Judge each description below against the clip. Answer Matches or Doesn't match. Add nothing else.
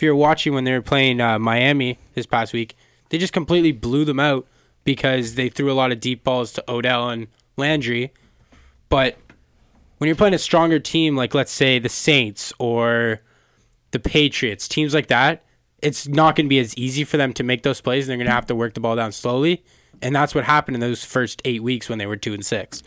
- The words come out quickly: Matches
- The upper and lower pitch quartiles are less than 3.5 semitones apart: Doesn't match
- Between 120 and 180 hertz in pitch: Matches